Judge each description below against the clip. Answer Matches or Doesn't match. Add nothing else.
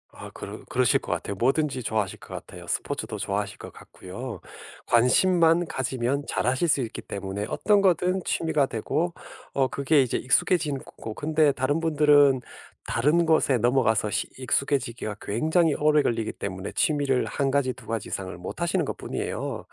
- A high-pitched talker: Doesn't match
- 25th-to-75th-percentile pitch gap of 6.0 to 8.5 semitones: Doesn't match